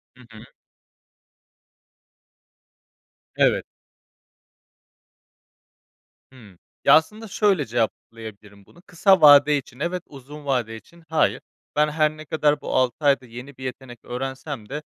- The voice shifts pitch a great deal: No, average, 4.0 semitones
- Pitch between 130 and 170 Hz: Yes, medium, 140 Hz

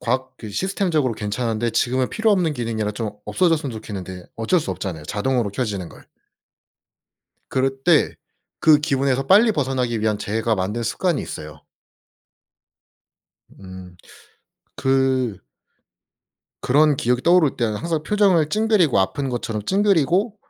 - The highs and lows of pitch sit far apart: Yes, wide, 6.6 semitones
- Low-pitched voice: Yes, low, 130 Hz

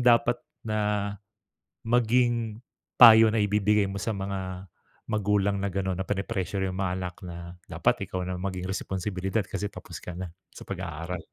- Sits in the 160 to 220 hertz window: No, low, 100 Hz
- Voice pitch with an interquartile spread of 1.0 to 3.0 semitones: Yes, narrow, 2.5 semitones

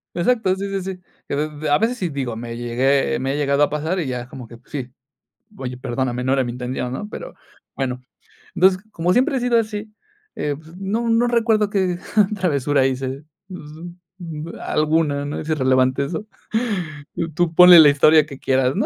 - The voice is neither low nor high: Yes, medium, 150 Hz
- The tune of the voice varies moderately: No, wide, 6.2 semitones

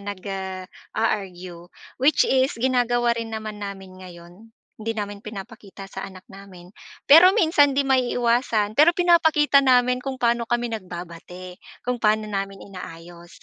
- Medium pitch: No, high, 215 Hz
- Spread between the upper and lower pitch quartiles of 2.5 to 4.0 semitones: No, average, 4.9 semitones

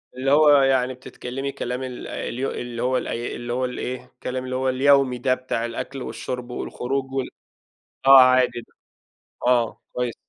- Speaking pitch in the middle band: No, low, 130 Hz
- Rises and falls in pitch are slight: Yes, narrow, 1.3 semitones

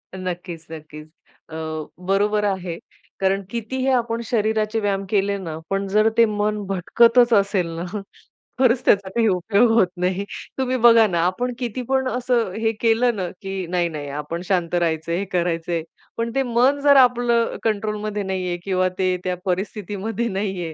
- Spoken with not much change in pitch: No, average, 4.1 semitones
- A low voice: No, high, 200 Hz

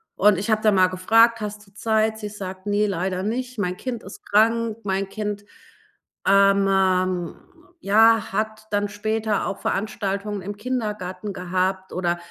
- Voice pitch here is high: Yes, high, 205 Hz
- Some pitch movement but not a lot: No, narrow, 2.3 semitones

